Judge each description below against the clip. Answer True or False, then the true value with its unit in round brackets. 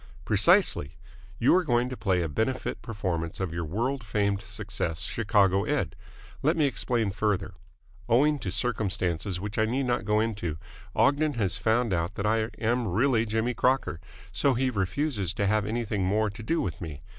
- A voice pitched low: True (110 Hz)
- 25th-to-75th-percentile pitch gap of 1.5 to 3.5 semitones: False (4.0 semitones)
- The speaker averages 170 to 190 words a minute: True (175 wpm)